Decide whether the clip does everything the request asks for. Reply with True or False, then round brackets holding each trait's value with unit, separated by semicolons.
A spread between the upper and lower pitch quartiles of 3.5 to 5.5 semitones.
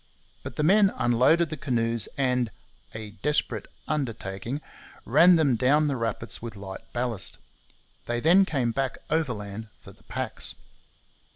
True (4.9 semitones)